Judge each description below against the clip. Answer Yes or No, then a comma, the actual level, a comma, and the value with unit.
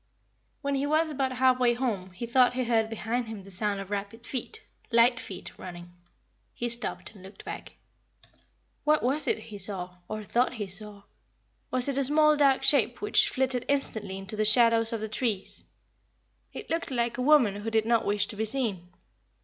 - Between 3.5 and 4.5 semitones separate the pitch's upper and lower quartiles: Yes, average, 4.0 semitones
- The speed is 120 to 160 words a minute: No, average, 190 wpm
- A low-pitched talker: No, high, 230 Hz